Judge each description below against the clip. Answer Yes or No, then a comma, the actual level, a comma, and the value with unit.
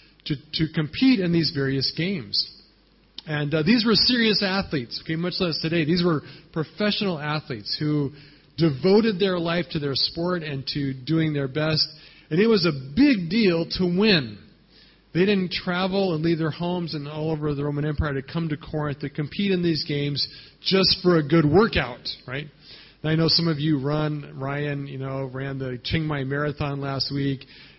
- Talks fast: No, average, 185 wpm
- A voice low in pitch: No, medium, 155 Hz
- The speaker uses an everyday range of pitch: Yes, average, 3.5 semitones